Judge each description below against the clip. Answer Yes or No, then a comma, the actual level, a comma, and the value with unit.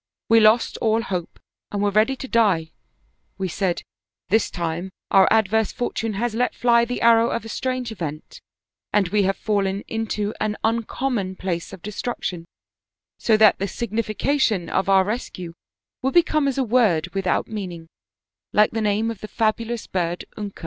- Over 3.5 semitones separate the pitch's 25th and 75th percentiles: No, average, 3.2 semitones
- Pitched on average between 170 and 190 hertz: No, high, 215 Hz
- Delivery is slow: No, average, 175 wpm